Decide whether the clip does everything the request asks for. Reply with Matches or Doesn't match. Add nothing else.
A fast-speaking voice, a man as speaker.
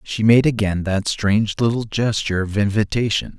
Doesn't match